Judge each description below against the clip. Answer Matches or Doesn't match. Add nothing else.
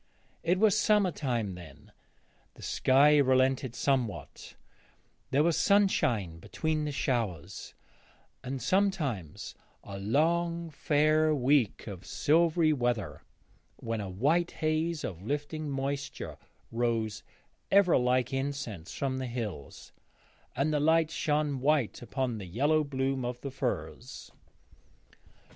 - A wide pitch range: Doesn't match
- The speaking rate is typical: Doesn't match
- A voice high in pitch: Doesn't match